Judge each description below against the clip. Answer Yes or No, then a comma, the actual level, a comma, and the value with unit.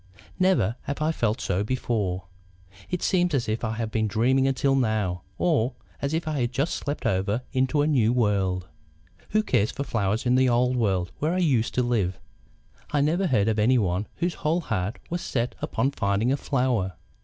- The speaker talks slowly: No, average, 190 wpm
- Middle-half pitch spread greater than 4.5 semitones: Yes, average, 5.0 semitones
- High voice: No, low, 120 Hz